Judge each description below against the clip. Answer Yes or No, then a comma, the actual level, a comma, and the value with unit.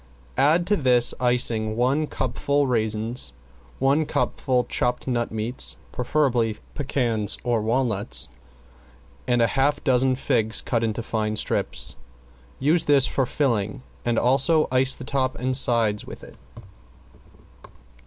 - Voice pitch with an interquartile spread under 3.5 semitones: Yes, average, 3.0 semitones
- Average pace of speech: No, slow, 130 wpm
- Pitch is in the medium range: No, low, 125 Hz